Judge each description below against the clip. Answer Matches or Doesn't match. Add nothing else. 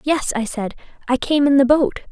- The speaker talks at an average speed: Doesn't match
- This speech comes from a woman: Matches